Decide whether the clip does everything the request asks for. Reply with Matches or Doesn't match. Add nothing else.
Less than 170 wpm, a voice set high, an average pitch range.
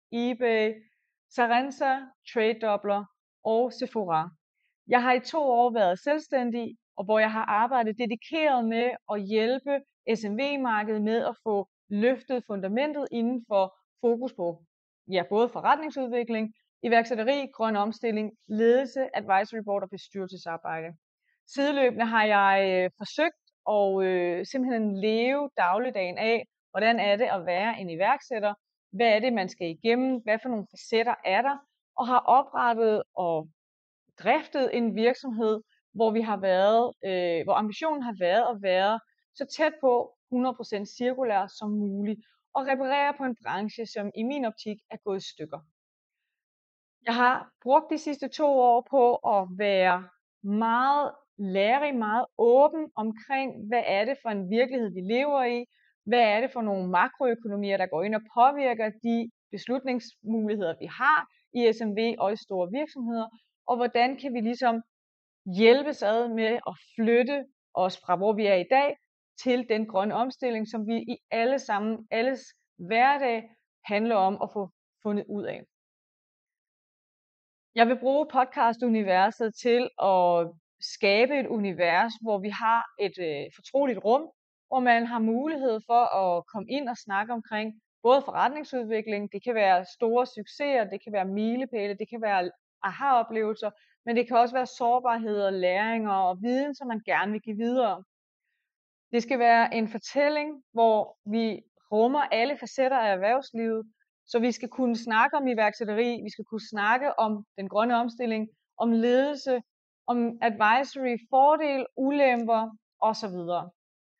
Matches